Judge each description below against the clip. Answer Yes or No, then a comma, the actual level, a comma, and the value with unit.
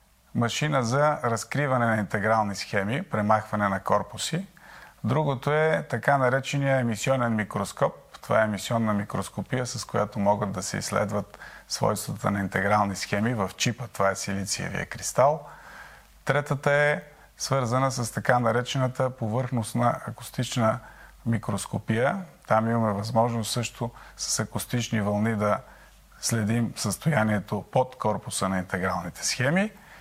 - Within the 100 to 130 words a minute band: Yes, average, 120 wpm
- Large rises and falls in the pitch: No, average, 3.7 semitones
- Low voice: Yes, low, 115 Hz